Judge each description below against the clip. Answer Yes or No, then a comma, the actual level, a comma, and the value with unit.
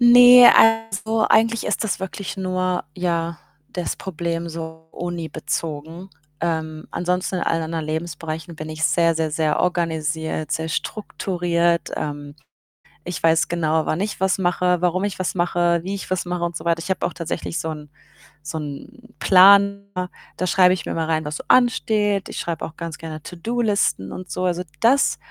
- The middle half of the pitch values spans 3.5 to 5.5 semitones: No, average, 2.9 semitones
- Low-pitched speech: No, medium, 175 Hz